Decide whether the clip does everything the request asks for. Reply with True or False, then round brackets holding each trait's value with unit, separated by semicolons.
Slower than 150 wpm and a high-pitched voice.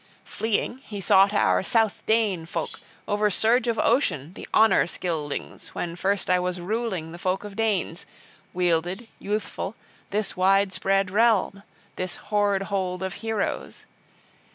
True (135 wpm; 195 Hz)